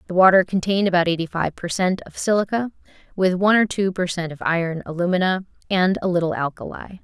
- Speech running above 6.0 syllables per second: Yes, 6.3 syllables/s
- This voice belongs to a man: No, female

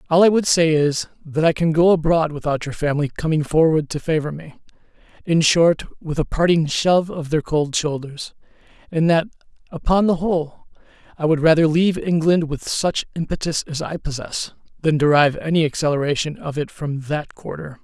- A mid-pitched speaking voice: Yes, medium, 155 Hz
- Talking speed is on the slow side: No, average, 175 wpm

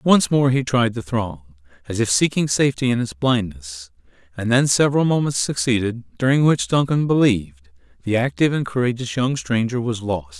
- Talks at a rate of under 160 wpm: No, average, 175 wpm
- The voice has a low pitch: Yes, low, 115 Hz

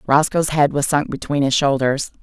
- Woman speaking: Yes, female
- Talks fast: No, average, 190 wpm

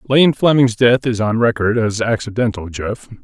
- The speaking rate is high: No, average, 165 wpm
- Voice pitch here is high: No, low, 115 Hz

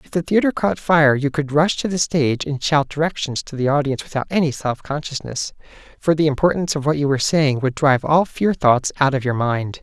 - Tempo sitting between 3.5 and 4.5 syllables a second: No, 5.8 syllables/s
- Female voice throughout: No, male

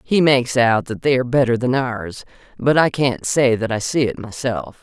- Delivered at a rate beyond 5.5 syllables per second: No, 5.0 syllables/s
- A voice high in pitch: No, low, 125 Hz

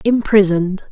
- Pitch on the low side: No, high, 200 Hz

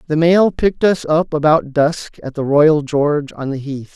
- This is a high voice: No, medium, 155 Hz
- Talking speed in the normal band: No, fast, 215 wpm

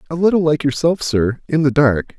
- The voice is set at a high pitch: No, medium, 145 Hz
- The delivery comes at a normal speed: Yes, average, 190 wpm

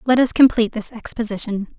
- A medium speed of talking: Yes, average, 170 wpm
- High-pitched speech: Yes, high, 230 Hz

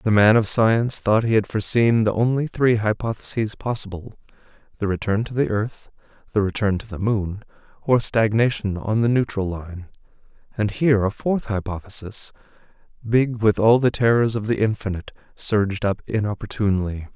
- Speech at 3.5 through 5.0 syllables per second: No, 5.3 syllables/s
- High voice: No, low, 110 Hz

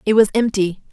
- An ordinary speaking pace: Yes, average, 195 wpm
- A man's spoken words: No, female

